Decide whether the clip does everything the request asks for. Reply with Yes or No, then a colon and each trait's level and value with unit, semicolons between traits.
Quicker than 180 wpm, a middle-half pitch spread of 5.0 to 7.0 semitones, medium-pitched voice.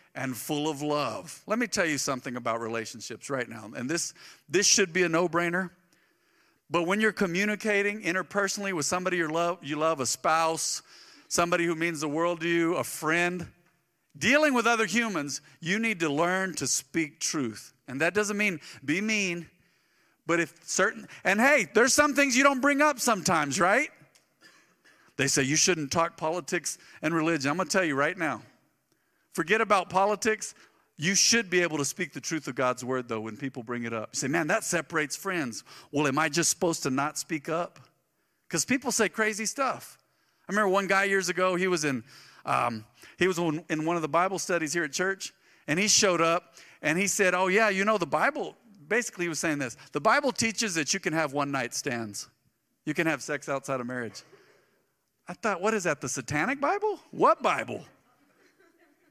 Yes: average, 195 wpm; average, 5.3 semitones; medium, 175 Hz